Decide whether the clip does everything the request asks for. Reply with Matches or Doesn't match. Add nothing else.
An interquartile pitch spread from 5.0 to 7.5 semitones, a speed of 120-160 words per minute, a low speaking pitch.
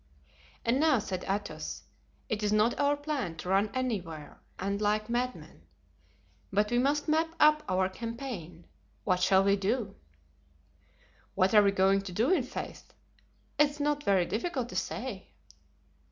Doesn't match